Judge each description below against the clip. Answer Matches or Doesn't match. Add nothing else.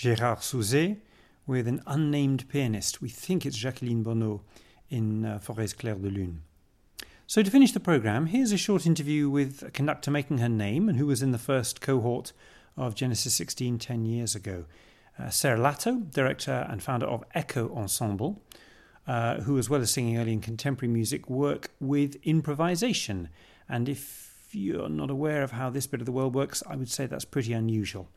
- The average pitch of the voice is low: Matches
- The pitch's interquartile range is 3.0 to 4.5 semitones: Matches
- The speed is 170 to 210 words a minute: Matches